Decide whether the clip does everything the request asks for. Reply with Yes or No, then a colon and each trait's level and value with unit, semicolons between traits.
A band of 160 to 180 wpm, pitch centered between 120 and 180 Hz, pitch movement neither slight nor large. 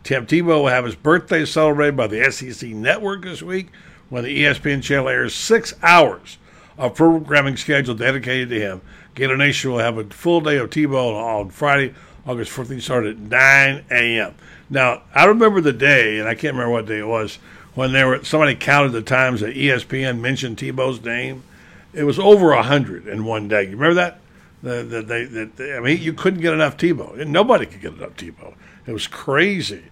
No: average, 195 wpm; low, 135 Hz; average, 4.2 semitones